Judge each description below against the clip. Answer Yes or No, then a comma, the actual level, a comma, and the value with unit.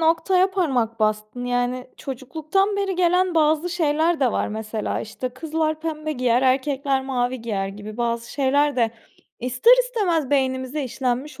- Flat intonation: No, average, 4.6 semitones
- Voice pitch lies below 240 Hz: No, very high, 270 Hz